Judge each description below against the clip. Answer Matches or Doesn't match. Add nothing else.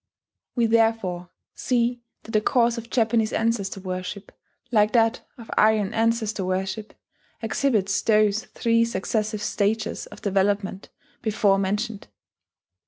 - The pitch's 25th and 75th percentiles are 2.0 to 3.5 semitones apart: Matches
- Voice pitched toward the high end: Matches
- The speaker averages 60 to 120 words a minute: Matches